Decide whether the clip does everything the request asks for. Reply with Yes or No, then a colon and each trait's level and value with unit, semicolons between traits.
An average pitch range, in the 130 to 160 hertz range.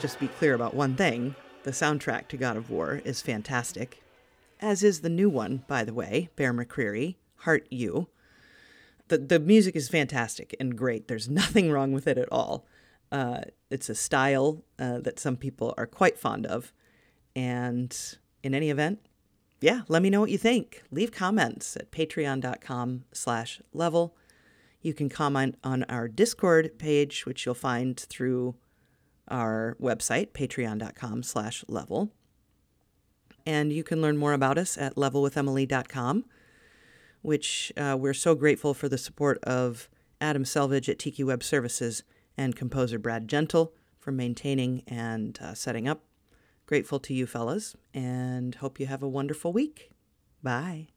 Yes: average, 3.8 semitones; low, 135 Hz